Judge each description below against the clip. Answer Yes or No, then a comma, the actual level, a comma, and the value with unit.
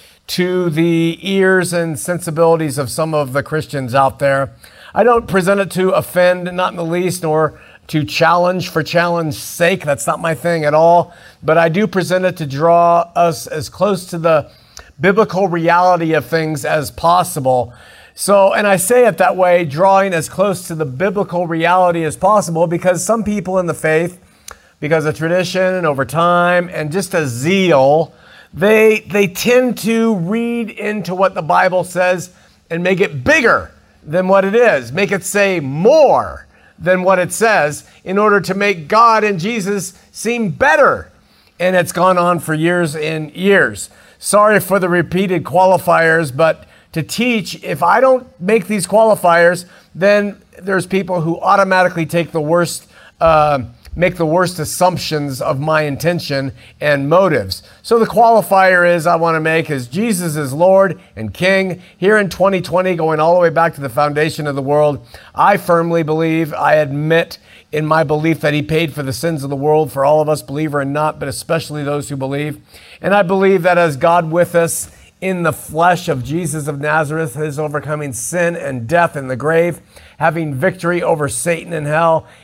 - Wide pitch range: No, average, 3.3 semitones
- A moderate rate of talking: Yes, average, 180 wpm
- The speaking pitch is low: No, medium, 170 Hz